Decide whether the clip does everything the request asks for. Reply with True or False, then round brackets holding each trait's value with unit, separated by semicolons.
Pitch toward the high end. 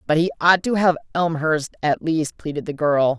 False (160 Hz)